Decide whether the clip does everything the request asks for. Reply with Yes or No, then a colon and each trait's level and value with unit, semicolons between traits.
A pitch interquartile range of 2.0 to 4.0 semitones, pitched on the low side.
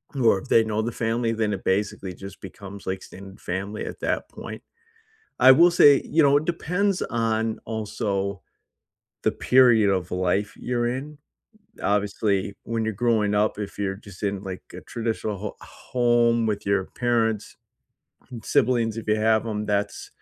Yes: average, 2.9 semitones; low, 110 Hz